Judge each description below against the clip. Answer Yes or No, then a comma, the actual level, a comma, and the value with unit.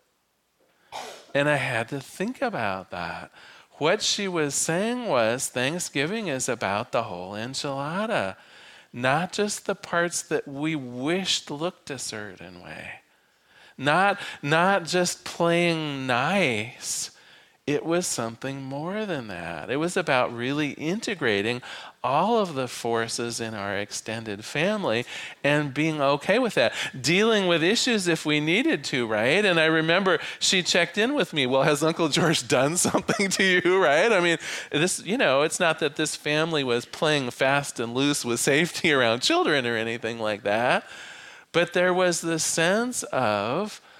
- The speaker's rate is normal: Yes, average, 155 wpm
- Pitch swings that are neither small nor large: No, wide, 5.8 semitones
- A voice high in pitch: No, medium, 155 Hz